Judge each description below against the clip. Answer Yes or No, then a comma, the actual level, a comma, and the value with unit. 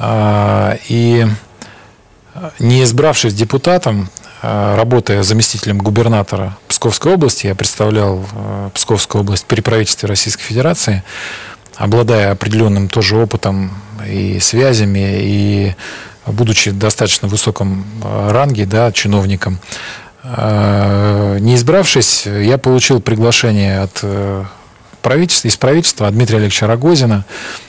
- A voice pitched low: Yes, low, 105 Hz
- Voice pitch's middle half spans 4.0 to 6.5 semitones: No, average, 2.8 semitones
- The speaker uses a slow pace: Yes, slow, 95 wpm